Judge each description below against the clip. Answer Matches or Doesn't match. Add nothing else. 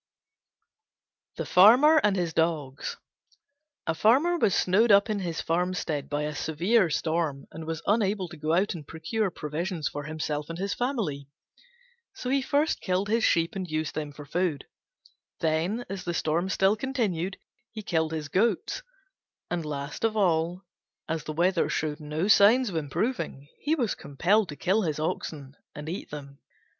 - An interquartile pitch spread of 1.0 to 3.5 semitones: Doesn't match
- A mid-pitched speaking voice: Matches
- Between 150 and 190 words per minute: Matches